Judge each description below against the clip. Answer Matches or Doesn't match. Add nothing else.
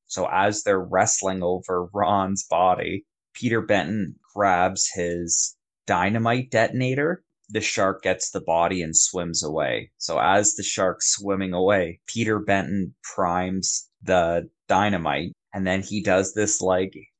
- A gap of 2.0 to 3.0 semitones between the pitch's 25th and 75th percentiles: Matches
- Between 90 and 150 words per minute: Matches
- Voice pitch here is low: Matches